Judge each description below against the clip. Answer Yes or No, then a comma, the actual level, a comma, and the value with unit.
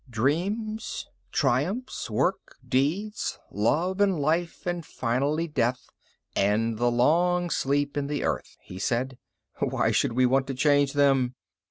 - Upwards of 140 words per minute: No, slow, 135 wpm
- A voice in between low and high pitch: Yes, medium, 145 Hz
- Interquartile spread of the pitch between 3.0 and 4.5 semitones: No, wide, 5.6 semitones